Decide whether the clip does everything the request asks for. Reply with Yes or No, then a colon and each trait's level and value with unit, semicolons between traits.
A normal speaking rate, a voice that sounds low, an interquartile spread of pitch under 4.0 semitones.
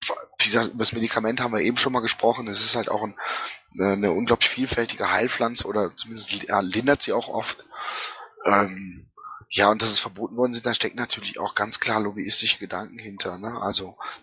Yes: average, 175 wpm; low, 110 Hz; narrow, 2.4 semitones